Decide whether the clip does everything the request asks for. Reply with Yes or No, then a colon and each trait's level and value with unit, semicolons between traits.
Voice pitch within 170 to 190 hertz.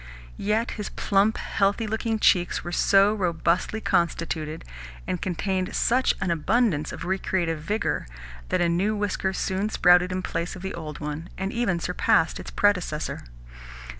Yes: medium, 185 Hz